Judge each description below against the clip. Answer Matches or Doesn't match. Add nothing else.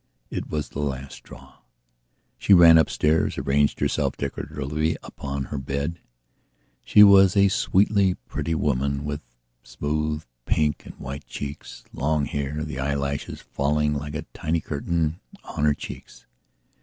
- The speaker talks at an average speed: Doesn't match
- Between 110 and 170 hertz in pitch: Doesn't match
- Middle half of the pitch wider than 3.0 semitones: Doesn't match